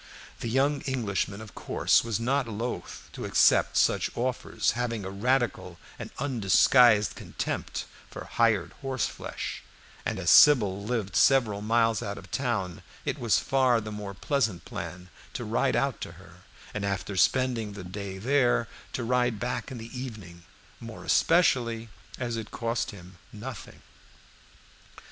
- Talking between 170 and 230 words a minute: No, average, 145 wpm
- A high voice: No, low, 115 Hz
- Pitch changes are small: No, average, 3.7 semitones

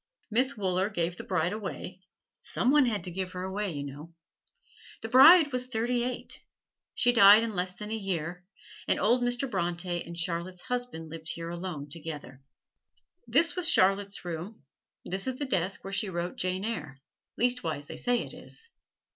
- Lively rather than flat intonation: Yes, wide, 5.8 semitones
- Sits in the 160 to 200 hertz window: Yes, high, 190 Hz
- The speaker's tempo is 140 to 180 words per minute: Yes, average, 175 wpm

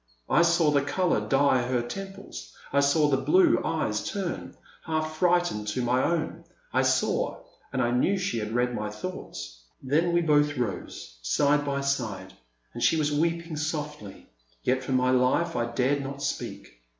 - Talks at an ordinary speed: Yes, average, 175 wpm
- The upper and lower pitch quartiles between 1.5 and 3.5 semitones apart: No, average, 5.0 semitones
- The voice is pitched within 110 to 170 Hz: Yes, medium, 140 Hz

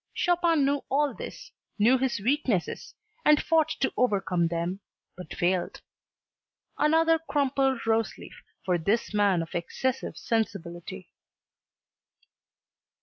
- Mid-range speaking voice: No, high, 230 Hz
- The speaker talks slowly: Yes, slow, 105 wpm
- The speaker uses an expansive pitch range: Yes, wide, 7.8 semitones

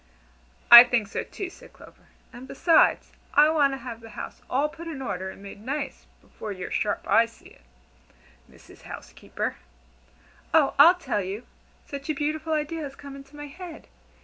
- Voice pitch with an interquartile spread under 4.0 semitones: No, average, 4.9 semitones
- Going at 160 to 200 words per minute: Yes, average, 175 wpm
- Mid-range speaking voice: No, very high, 275 Hz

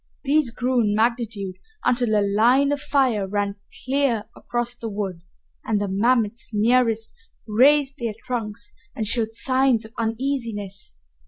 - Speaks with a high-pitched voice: Yes, high, 230 Hz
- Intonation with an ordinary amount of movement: Yes, average, 3.4 semitones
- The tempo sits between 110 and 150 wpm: Yes, average, 140 wpm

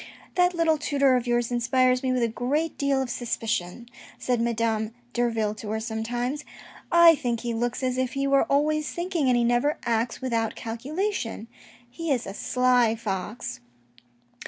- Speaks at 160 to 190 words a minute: Yes, average, 175 wpm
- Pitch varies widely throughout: No, average, 3.2 semitones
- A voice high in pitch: Yes, high, 245 Hz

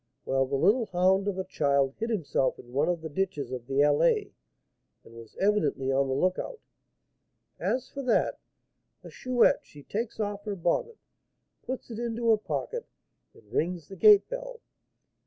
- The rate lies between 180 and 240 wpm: No, average, 170 wpm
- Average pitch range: No, wide, 8.7 semitones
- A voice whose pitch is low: No, high, 190 Hz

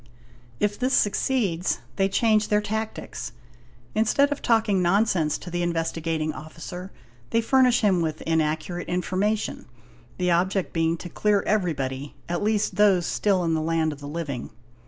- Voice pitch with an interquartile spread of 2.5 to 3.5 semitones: No, average, 4.3 semitones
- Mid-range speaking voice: Yes, medium, 180 Hz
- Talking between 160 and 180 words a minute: No, average, 150 wpm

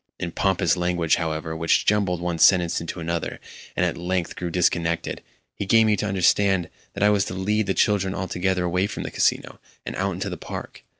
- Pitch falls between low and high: No, very low, 90 Hz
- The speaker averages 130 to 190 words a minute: No, average, 200 wpm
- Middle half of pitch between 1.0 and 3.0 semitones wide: Yes, narrow, 2.4 semitones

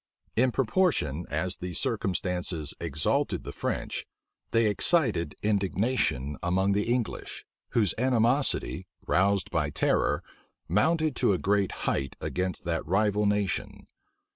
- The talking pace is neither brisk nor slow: No, slow, 115 wpm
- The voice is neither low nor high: No, low, 100 Hz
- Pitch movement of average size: Yes, average, 4.8 semitones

